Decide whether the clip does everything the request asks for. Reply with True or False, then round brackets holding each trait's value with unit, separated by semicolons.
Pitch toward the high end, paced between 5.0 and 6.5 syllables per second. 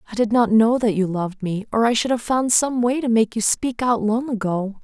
True (225 Hz; 5.3 syllables/s)